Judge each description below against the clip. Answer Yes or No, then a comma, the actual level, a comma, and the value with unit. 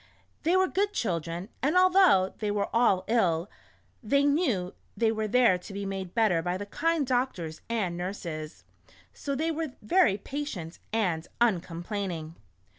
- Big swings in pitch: Yes, wide, 7.5 semitones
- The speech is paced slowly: No, average, 150 wpm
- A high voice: Yes, high, 210 Hz